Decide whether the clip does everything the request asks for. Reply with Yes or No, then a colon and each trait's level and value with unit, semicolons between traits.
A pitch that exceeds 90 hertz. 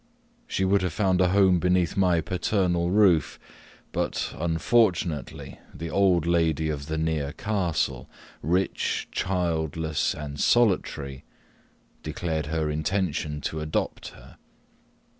No: very low, 85 Hz